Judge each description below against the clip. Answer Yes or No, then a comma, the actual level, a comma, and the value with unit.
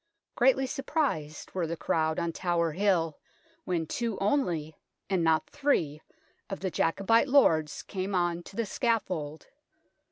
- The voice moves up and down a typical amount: No, wide, 6.0 semitones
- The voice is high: No, medium, 180 Hz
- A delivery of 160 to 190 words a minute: No, slow, 135 wpm